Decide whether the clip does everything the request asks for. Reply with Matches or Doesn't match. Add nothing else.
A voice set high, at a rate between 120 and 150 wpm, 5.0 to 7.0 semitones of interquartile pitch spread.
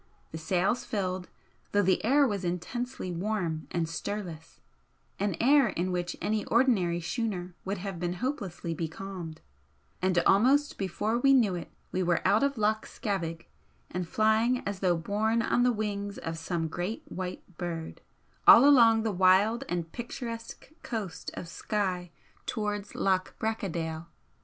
Doesn't match